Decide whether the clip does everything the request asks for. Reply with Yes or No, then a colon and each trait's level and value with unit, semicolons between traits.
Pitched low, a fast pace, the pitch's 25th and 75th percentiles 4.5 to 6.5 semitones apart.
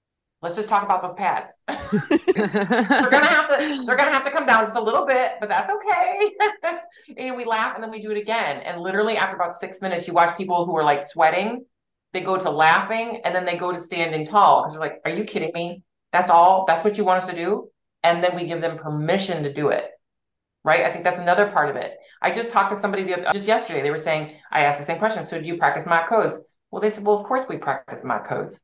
No: high, 190 Hz; fast, 260 wpm; average, 5.2 semitones